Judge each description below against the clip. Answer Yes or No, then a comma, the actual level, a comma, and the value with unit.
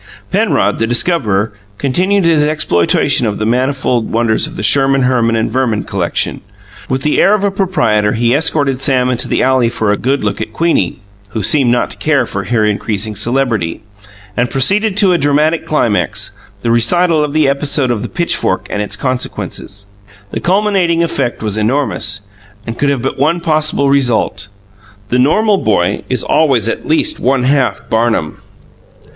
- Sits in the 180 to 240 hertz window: No, low, 130 Hz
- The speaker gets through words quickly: No, average, 170 wpm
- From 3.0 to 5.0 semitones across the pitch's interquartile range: No, wide, 5.4 semitones